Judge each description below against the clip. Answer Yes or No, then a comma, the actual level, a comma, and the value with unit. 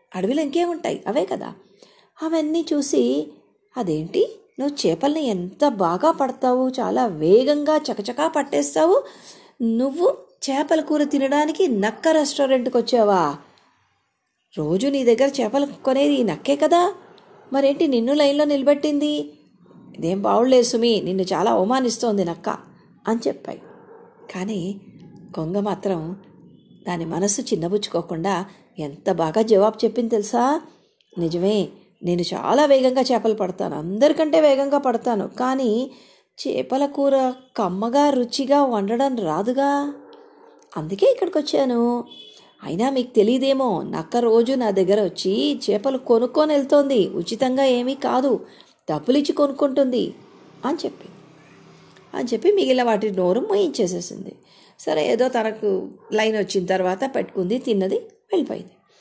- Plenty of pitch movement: Yes, wide, 6.1 semitones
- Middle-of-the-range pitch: No, very high, 250 Hz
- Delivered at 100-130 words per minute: Yes, average, 110 wpm